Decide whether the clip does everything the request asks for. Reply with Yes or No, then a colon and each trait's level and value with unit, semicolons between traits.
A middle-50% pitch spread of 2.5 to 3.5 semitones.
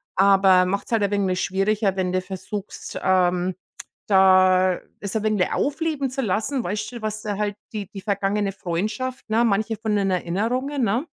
Yes: average, 2.8 semitones